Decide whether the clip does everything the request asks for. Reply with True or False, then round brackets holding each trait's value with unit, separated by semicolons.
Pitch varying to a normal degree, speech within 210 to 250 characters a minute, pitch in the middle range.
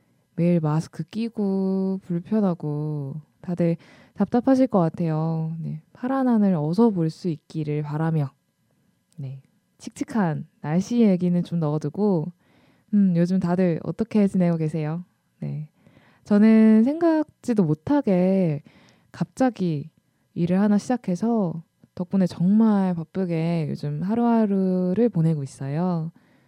True (4.5 semitones; 240 characters per minute; 180 Hz)